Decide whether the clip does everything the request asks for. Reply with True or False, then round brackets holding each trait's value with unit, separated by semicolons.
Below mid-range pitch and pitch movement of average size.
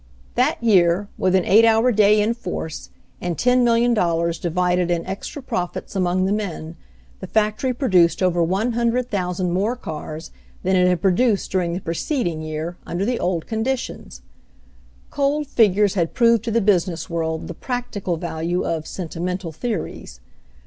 False (185 Hz; 4.8 semitones)